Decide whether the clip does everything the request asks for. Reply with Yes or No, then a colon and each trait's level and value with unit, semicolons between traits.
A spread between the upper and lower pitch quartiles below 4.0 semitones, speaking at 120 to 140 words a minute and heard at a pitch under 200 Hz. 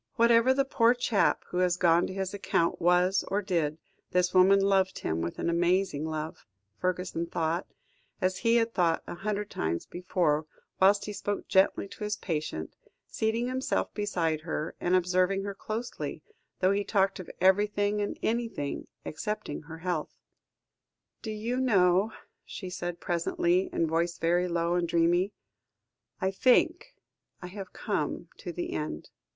No: average, 3.3 semitones; average, 155 wpm; medium, 185 Hz